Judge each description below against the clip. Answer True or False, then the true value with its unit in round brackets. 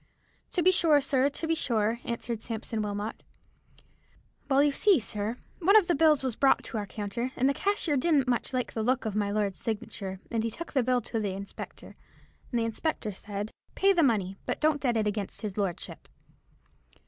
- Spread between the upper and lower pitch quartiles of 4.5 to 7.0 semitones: True (5.3 semitones)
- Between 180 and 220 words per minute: True (200 wpm)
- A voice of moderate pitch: False (235 Hz)